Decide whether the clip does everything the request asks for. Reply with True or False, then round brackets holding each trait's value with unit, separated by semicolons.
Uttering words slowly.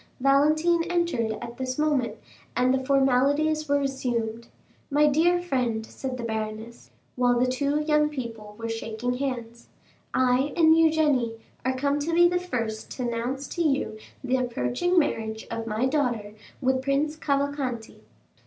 False (150 wpm)